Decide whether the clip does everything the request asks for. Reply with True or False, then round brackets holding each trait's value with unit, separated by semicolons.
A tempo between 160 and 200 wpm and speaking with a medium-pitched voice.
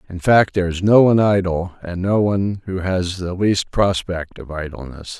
False (195 wpm; 90 Hz)